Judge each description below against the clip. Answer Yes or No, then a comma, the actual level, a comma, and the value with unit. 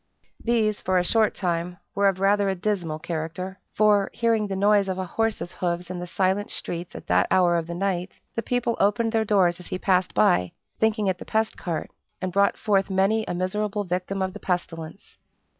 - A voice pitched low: No, high, 190 Hz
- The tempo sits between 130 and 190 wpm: No, fast, 205 wpm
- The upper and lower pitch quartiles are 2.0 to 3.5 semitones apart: Yes, average, 2.8 semitones